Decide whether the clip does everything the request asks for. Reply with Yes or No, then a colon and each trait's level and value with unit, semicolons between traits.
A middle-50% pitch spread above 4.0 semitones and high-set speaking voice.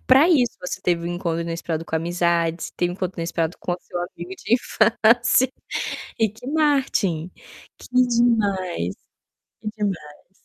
No: wide, 5.4 semitones; medium, 180 Hz